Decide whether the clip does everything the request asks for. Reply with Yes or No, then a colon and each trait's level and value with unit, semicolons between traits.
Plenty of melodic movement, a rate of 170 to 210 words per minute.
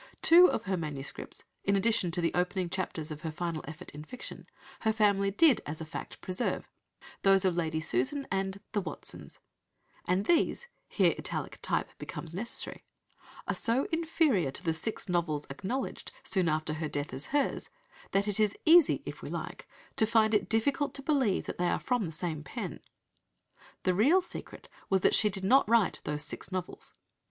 Yes: wide, 5.8 semitones; average, 180 wpm